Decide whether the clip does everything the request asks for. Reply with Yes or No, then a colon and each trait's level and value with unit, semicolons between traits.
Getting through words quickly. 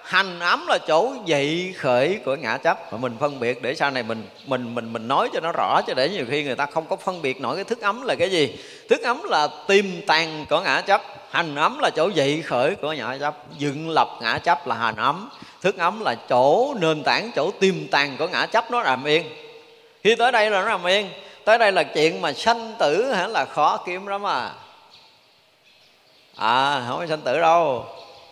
No: average, 225 wpm